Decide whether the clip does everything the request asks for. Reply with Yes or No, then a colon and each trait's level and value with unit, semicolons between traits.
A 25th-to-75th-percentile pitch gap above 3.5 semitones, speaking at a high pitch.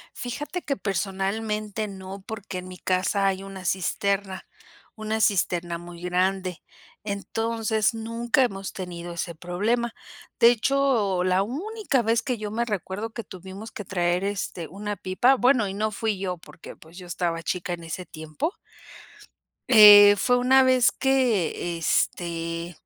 Yes: average, 3.9 semitones; high, 200 Hz